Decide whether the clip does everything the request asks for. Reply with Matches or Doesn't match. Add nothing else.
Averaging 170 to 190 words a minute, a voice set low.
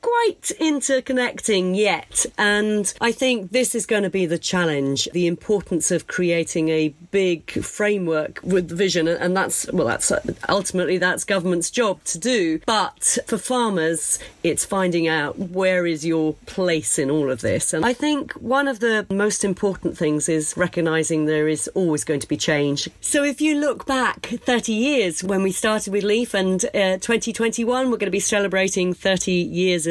Doesn't match